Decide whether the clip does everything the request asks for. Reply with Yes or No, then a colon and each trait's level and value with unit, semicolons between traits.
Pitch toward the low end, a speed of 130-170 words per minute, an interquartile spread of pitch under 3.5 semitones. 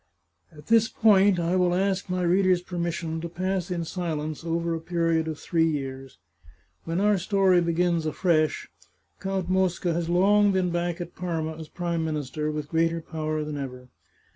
No: medium, 170 Hz; average, 165 wpm; narrow, 2.4 semitones